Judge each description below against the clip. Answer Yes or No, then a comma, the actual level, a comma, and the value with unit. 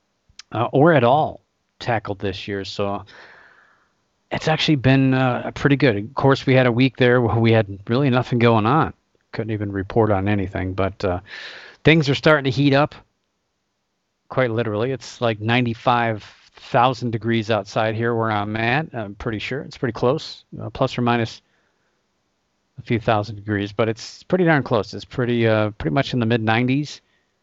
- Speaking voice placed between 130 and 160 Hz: No, low, 115 Hz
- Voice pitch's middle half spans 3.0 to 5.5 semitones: Yes, average, 3.6 semitones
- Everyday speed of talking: Yes, average, 175 wpm